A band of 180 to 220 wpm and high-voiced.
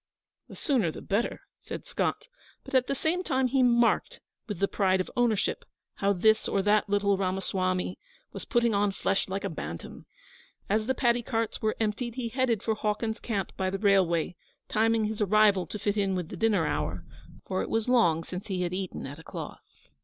Yes: average, 200 wpm; high, 205 Hz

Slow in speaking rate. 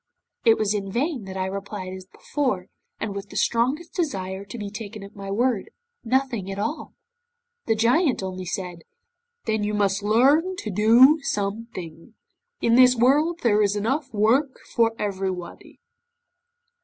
No: average, 155 wpm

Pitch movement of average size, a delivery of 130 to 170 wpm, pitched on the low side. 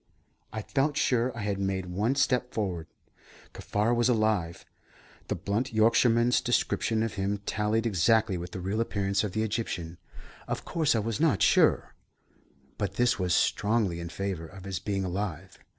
Yes: average, 3.5 semitones; average, 165 wpm; low, 105 Hz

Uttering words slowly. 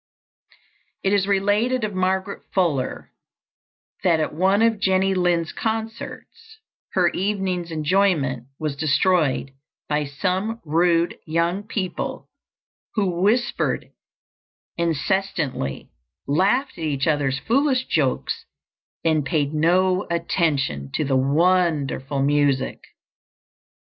Yes: slow, 100 wpm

